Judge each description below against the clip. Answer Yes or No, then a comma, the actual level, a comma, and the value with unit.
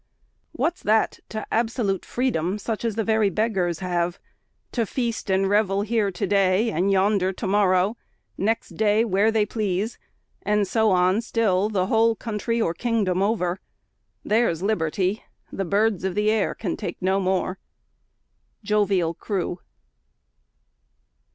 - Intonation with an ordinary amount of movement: Yes, average, 3.0 semitones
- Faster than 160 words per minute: No, average, 140 wpm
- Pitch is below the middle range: No, high, 205 Hz